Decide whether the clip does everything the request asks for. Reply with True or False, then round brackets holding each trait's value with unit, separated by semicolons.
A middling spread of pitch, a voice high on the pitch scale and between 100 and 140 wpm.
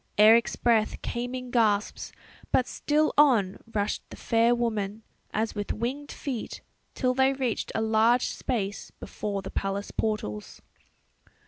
True (3.3 semitones; 225 Hz; 135 wpm)